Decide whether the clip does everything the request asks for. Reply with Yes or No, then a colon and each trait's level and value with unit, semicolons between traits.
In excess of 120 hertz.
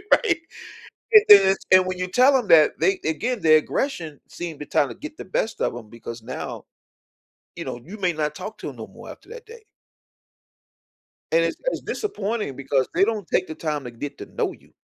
Yes: medium, 185 Hz